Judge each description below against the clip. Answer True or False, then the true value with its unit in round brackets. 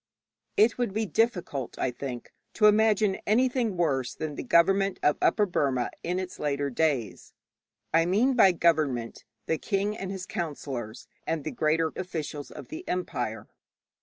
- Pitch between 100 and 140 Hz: False (170 Hz)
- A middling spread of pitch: False (6.3 semitones)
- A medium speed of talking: True (160 wpm)